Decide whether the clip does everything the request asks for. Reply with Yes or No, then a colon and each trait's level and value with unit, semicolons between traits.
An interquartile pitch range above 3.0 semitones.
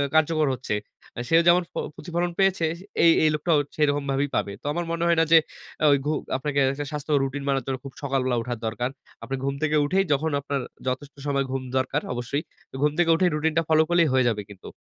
Yes: average, 3.4 semitones